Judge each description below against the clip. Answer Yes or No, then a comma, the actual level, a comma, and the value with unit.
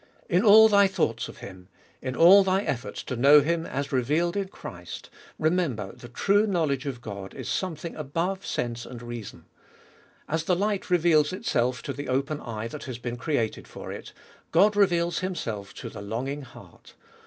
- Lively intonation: Yes, wide, 7.1 semitones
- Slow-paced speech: No, average, 175 wpm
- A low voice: No, medium, 145 Hz